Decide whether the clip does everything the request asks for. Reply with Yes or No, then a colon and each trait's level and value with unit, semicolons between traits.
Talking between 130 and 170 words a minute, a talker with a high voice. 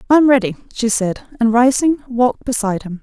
No: average, 200 wpm; high, 240 Hz